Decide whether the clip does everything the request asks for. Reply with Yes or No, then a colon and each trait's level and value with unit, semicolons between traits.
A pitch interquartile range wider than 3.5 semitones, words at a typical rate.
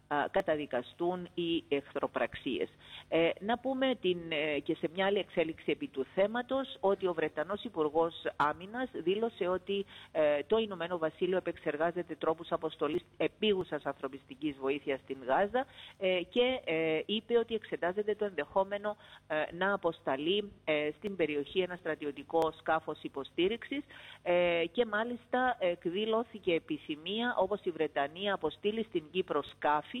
Yes: average, 5.1 semitones; average, 130 wpm